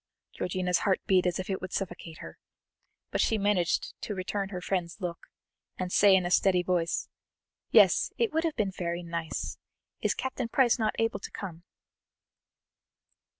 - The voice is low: No, medium, 185 Hz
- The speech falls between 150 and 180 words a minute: Yes, average, 165 wpm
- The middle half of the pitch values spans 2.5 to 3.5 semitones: Yes, average, 2.8 semitones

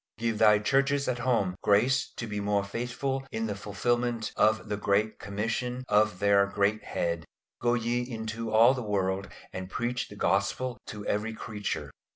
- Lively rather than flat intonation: No, average, 3.1 semitones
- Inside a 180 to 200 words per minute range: No, average, 170 wpm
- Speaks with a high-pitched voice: No, low, 110 Hz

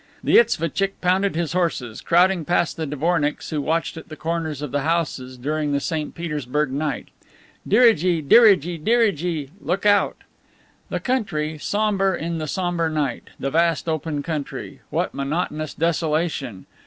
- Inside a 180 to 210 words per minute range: No, average, 145 wpm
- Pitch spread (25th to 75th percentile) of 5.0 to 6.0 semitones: No, average, 3.1 semitones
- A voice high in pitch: No, medium, 160 Hz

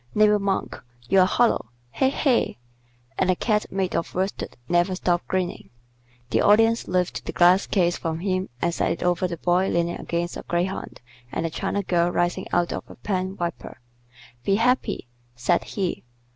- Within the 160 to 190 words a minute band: Yes, average, 170 wpm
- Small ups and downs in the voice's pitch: Yes, narrow, 2.3 semitones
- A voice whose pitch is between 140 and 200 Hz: Yes, medium, 185 Hz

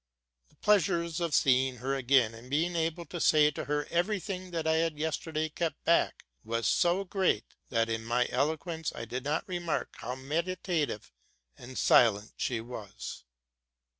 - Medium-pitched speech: Yes, medium, 150 Hz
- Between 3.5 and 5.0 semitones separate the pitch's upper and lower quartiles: No, wide, 5.4 semitones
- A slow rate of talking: No, average, 165 wpm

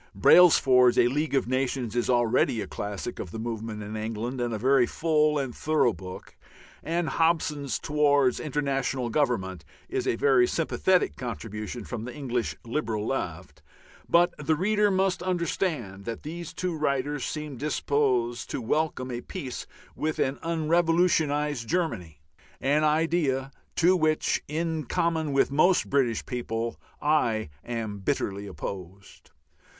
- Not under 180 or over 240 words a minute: No, average, 140 wpm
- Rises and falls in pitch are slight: No, average, 5.1 semitones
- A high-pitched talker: No, low, 135 Hz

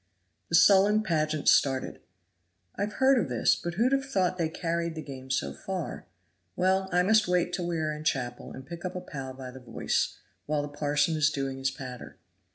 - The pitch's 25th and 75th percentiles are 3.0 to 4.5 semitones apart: No, average, 5.2 semitones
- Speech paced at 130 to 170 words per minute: No, average, 200 wpm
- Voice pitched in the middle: Yes, medium, 160 Hz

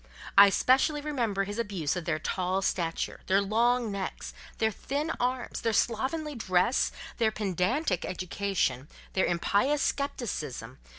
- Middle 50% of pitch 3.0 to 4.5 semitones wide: No, wide, 5.4 semitones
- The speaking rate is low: Yes, slow, 130 wpm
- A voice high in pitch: Yes, high, 205 Hz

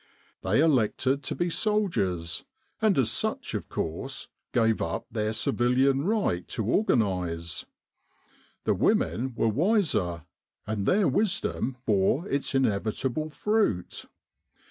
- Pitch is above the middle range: No, low, 125 Hz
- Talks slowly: Yes, slow, 115 wpm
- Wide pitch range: Yes, wide, 8.7 semitones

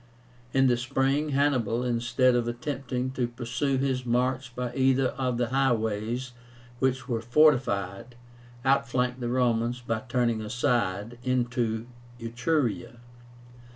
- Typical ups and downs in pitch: No, narrow, 1.9 semitones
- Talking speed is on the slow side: Yes, slow, 120 wpm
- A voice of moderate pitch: No, low, 125 Hz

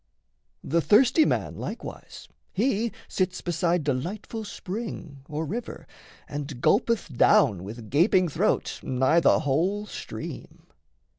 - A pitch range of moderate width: No, wide, 6.5 semitones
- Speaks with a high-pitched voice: No, medium, 170 Hz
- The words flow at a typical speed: No, slow, 115 wpm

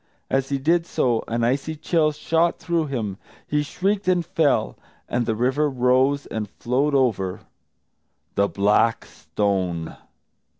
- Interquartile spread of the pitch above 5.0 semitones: Yes, wide, 5.5 semitones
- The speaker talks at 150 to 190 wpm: No, slow, 135 wpm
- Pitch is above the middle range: No, low, 135 Hz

